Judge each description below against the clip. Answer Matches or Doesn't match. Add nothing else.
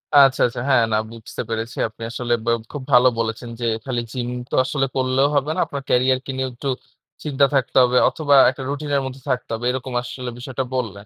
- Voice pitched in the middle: Doesn't match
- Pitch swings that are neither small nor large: Doesn't match